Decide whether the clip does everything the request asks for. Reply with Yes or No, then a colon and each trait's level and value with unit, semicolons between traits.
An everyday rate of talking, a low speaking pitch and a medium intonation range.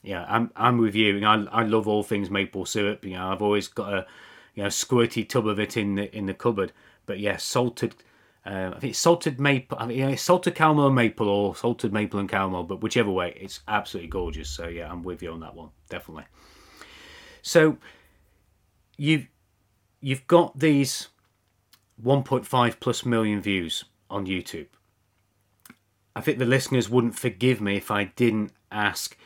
Yes: average, 180 wpm; low, 105 Hz; average, 4.2 semitones